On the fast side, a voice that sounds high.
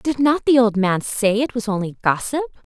Yes: fast, 215 wpm; high, 230 Hz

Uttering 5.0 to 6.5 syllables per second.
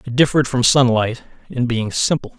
Yes: 5.5 syllables/s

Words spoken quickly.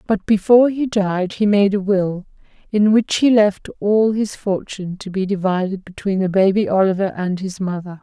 No: average, 185 wpm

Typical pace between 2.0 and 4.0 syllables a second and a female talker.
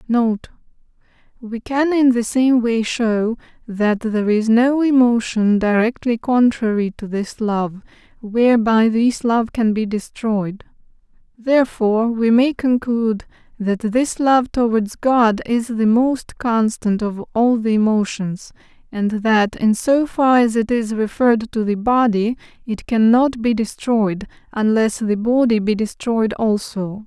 Yes: 3.9 syllables/s; female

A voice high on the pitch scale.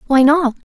Yes: very high, 280 Hz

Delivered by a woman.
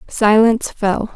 Yes: female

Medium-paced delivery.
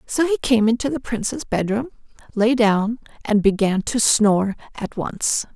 Yes: average, 160 wpm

